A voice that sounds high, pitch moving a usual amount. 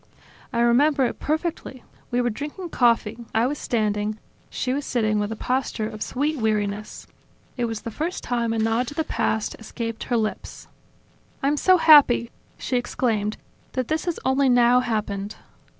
Yes: high, 240 Hz; average, 3.9 semitones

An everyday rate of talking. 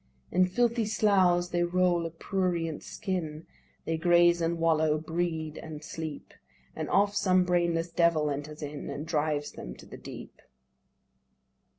Yes: average, 145 wpm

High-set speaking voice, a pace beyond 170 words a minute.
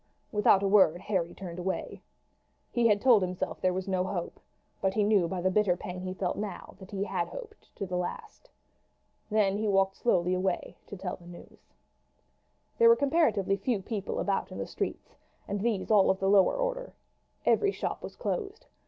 Yes: high, 195 Hz; average, 190 wpm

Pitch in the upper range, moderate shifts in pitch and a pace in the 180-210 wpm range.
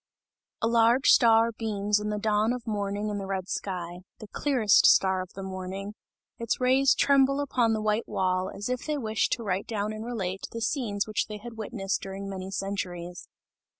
Yes: high, 210 Hz; average, 3.0 semitones; average, 190 wpm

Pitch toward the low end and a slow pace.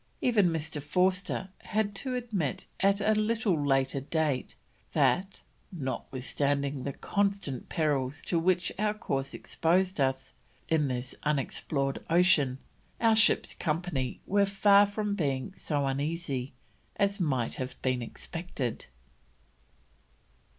No: medium, 160 Hz; slow, 115 wpm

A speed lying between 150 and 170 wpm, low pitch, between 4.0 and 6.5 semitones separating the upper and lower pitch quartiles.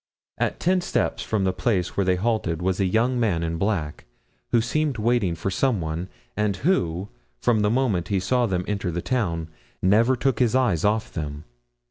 No: average, 190 wpm; low, 100 Hz; average, 5.2 semitones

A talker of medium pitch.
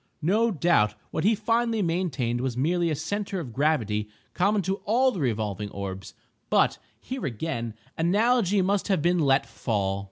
Yes: medium, 165 Hz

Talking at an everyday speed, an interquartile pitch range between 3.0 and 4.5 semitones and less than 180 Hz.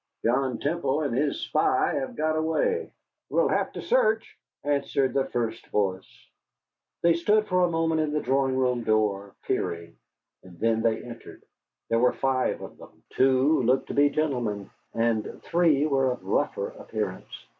No: average, 160 wpm; average, 5.3 semitones; low, 135 Hz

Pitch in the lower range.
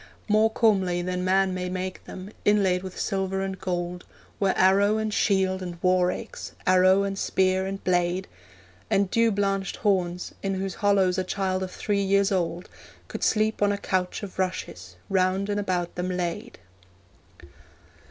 No: high, 190 Hz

